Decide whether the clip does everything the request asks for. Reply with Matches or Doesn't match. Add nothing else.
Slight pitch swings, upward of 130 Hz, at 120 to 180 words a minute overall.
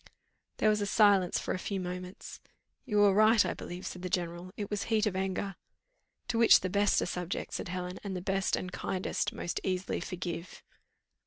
Doesn't match